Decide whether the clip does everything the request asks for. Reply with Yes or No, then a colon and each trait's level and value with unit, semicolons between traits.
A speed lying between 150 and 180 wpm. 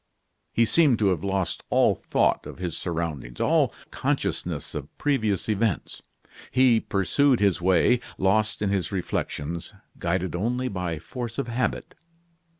No: average, 140 wpm